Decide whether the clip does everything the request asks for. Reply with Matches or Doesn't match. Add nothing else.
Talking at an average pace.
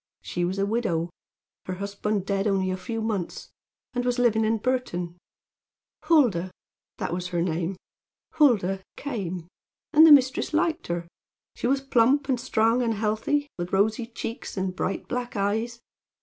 Matches